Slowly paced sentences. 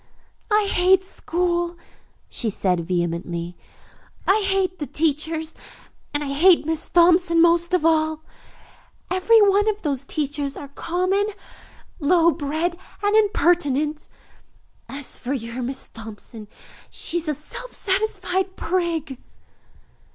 Yes: slow, 120 wpm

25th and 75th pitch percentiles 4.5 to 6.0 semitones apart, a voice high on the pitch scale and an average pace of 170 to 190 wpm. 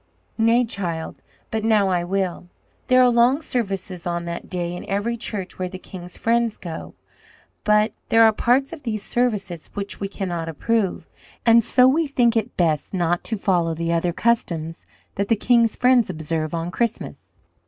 Yes: average, 5.1 semitones; high, 200 Hz; average, 175 wpm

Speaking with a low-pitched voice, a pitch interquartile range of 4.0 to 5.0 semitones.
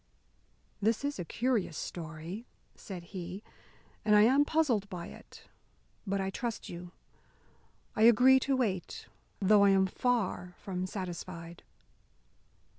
No: high, 195 Hz; average, 4.6 semitones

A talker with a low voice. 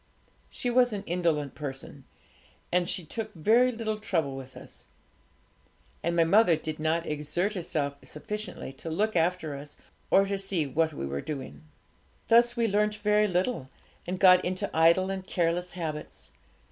No: medium, 175 Hz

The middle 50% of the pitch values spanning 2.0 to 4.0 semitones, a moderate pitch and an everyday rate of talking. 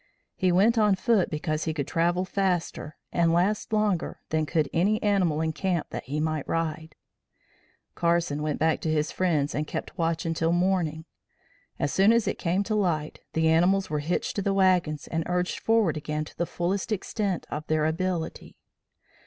Yes: average, 3.3 semitones; medium, 170 Hz; average, 180 wpm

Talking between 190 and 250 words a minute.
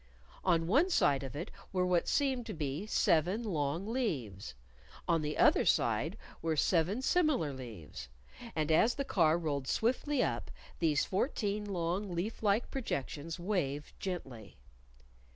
No: average, 140 wpm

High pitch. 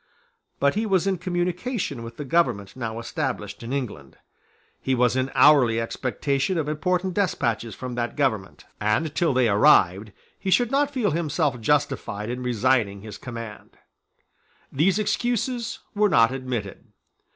No: low, 135 Hz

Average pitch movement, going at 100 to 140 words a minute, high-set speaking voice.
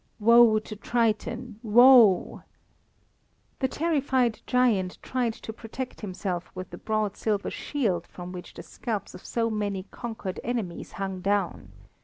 Yes: average, 3.9 semitones; slow, 135 wpm; high, 215 Hz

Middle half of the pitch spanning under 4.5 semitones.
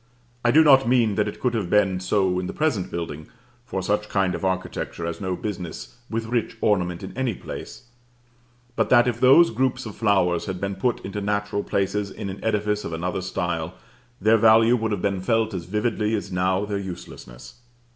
Yes: average, 3.4 semitones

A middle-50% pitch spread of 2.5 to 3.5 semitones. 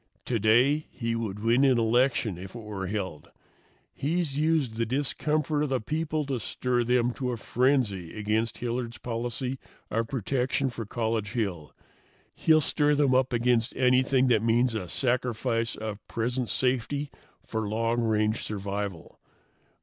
Yes: average, 3.1 semitones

